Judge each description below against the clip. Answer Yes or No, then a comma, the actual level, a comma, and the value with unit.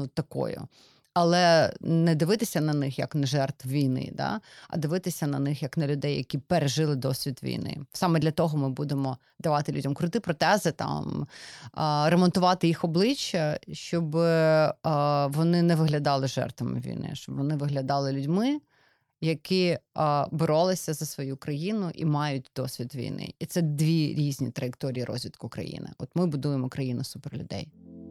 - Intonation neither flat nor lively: Yes, average, 3.3 semitones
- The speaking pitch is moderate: Yes, medium, 150 Hz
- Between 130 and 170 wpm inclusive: Yes, average, 145 wpm